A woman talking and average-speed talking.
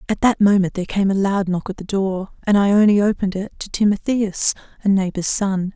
No: female; fast, 210 wpm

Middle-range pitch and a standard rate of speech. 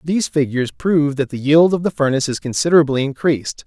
Yes: medium, 145 Hz; average, 195 wpm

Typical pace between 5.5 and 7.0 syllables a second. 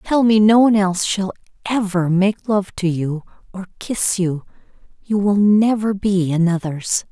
No: 4.5 syllables/s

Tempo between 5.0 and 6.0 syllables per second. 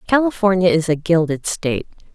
Yes: 5.7 syllables/s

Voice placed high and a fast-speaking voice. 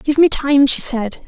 Yes: very high, 270 Hz; fast, 235 wpm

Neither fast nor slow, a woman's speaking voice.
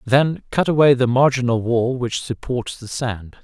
No: average, 175 wpm; male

